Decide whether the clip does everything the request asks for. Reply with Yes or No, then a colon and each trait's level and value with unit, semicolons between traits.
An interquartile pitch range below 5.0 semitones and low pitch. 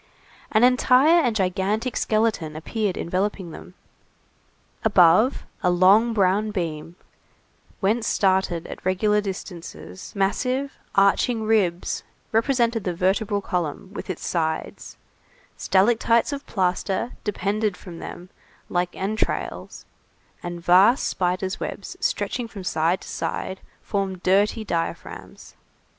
No: average, 3.6 semitones; high, 195 Hz